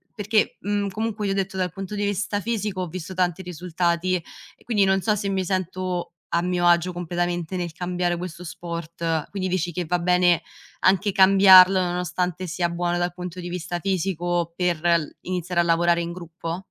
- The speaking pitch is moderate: Yes, medium, 180 Hz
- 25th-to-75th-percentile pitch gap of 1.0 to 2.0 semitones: Yes, narrow, 1.6 semitones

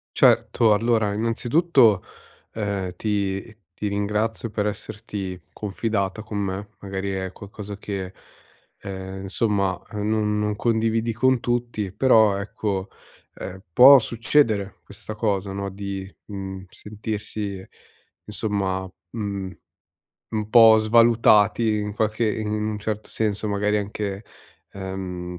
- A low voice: Yes, low, 105 Hz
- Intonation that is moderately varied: No, narrow, 2.0 semitones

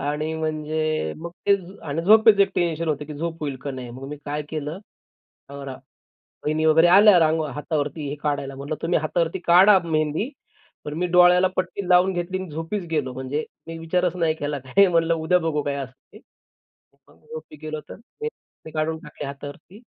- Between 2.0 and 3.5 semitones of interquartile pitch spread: Yes, average, 3.2 semitones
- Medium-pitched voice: Yes, medium, 160 Hz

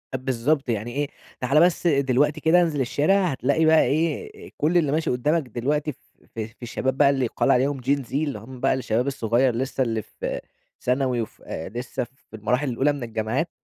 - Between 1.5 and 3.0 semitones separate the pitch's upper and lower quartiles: No, average, 3.5 semitones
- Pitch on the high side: No, low, 135 Hz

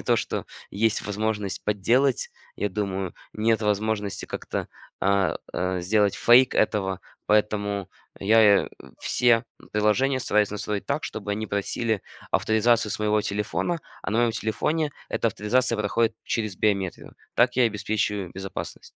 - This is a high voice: No, low, 105 Hz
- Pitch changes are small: Yes, narrow, 2.1 semitones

